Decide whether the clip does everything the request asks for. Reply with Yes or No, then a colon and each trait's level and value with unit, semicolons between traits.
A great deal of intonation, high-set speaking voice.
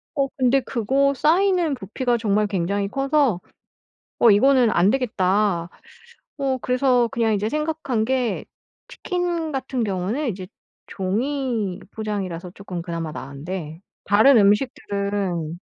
Yes: wide, 5.8 semitones; high, 220 Hz